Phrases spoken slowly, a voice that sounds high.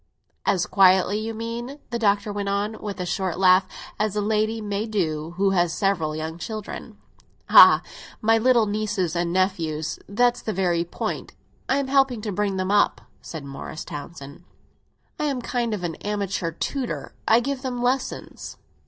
No: average, 165 wpm; high, 205 Hz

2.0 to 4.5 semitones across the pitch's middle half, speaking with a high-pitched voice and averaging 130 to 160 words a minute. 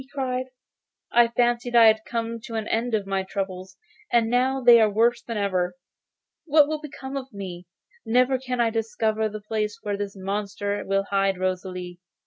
No: average, 3.6 semitones; high, 220 Hz; average, 180 wpm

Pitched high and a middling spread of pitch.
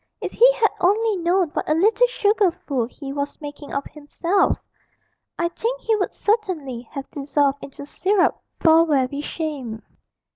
No: very high, 320 Hz; wide, 6.2 semitones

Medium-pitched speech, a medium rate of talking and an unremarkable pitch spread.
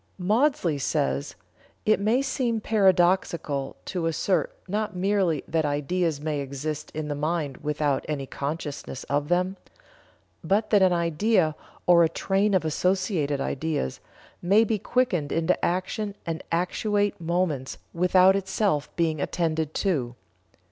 No: medium, 170 Hz; slow, 130 wpm; average, 4.4 semitones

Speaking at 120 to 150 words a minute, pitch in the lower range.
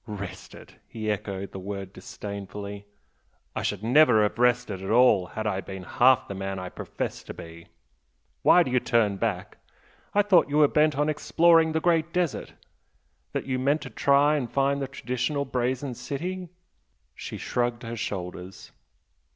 No: average, 165 wpm; low, 120 Hz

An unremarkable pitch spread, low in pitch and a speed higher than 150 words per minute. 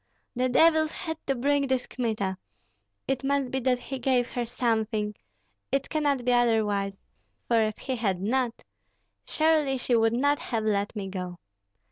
No: average, 3.7 semitones; high, 245 Hz; average, 160 wpm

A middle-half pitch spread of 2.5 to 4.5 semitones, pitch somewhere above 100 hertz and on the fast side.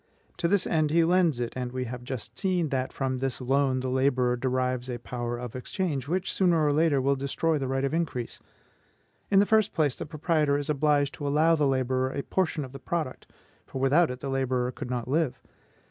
Yes: average, 3.7 semitones; low, 135 Hz; fast, 215 wpm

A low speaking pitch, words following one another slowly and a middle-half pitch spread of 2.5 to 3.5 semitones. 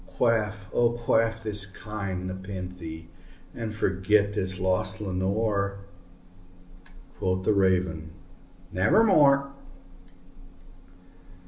Yes: low, 100 Hz; slow, 80 wpm; average, 2.9 semitones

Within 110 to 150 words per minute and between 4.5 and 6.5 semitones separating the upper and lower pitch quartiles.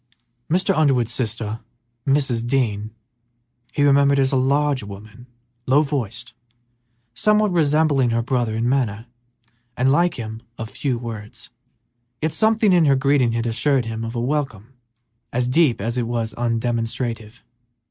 No: average, 140 wpm; average, 3.7 semitones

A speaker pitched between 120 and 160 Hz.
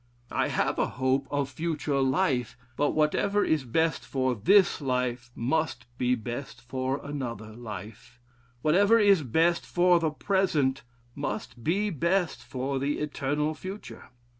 Yes: medium, 140 Hz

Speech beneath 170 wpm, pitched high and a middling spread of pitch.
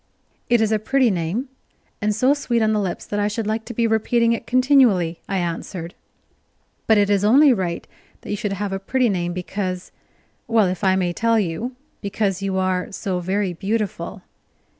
No: average, 190 wpm; high, 205 Hz; average, 3.6 semitones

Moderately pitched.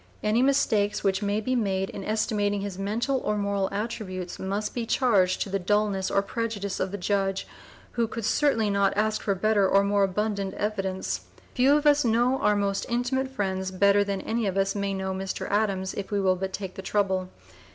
No: high, 200 Hz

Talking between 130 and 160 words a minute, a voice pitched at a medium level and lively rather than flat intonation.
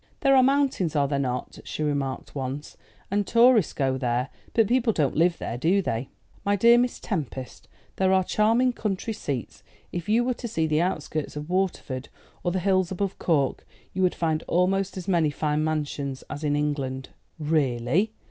No: average, 180 wpm; medium, 165 Hz; wide, 5.9 semitones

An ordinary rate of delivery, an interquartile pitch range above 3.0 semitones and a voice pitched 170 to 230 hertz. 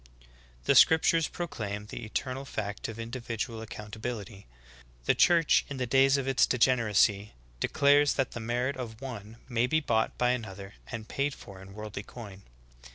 No: average, 175 wpm; average, 4.0 semitones; low, 115 Hz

